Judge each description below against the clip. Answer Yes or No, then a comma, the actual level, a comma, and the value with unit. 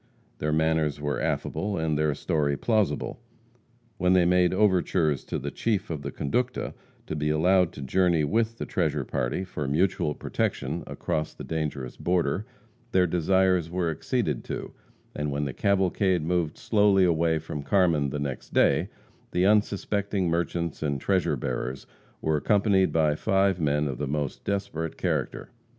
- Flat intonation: No, average, 4.1 semitones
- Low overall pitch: Yes, very low, 85 Hz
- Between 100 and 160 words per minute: Yes, average, 155 wpm